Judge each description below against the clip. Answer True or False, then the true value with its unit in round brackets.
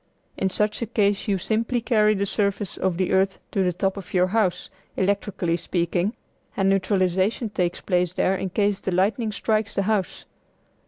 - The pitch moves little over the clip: True (2.3 semitones)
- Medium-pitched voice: False (195 Hz)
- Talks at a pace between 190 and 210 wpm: False (175 wpm)